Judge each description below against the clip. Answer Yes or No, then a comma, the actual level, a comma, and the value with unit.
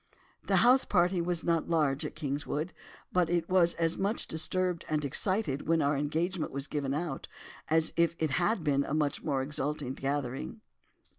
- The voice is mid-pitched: Yes, medium, 160 Hz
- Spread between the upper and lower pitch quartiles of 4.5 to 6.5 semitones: No, average, 3.3 semitones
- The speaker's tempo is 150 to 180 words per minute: Yes, average, 170 wpm